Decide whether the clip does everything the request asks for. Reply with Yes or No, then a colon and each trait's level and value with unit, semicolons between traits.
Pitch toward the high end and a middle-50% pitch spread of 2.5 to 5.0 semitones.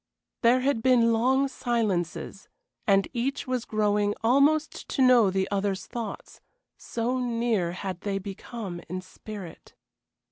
Yes: high, 225 Hz; average, 4.3 semitones